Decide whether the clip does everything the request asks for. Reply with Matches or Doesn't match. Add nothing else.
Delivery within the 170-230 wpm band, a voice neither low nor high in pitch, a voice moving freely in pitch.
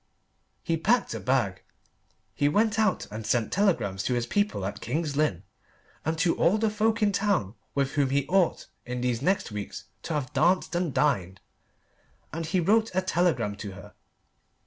Matches